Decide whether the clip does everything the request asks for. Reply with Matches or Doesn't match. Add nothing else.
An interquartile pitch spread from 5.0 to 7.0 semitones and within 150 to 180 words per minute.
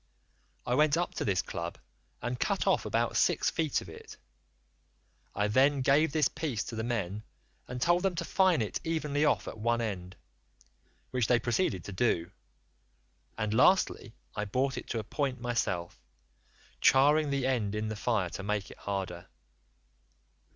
Matches